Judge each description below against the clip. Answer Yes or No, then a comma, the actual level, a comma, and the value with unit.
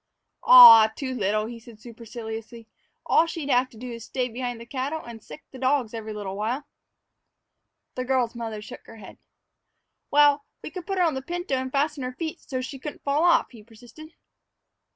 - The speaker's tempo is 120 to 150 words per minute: No, average, 195 wpm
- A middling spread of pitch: Yes, average, 4.0 semitones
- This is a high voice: Yes, very high, 255 Hz